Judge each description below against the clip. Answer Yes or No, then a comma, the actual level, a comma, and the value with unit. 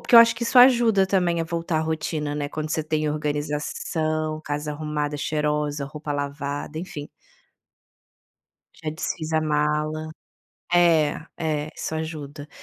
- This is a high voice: No, medium, 155 Hz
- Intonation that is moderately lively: No, narrow, 1.5 semitones